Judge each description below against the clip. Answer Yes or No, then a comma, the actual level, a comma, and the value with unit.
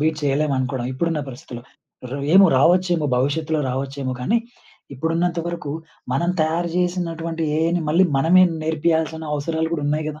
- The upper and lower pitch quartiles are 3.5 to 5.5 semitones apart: No, average, 2.9 semitones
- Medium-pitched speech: Yes, medium, 160 Hz